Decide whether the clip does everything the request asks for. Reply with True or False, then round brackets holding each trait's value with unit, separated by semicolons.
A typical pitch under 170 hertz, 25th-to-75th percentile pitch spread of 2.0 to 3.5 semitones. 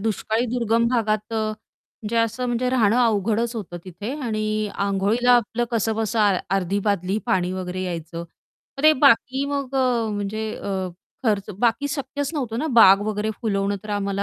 False (220 Hz; 3.2 semitones)